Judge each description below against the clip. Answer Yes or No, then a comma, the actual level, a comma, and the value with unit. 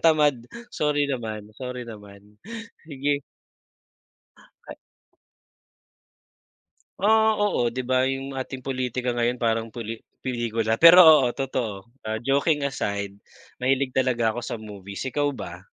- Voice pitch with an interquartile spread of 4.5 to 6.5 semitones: No, average, 3.7 semitones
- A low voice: Yes, low, 125 Hz